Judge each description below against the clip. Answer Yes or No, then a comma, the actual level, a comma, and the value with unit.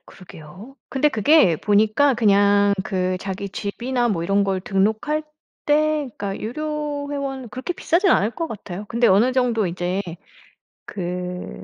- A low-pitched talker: No, high, 215 Hz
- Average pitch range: No, wide, 6.1 semitones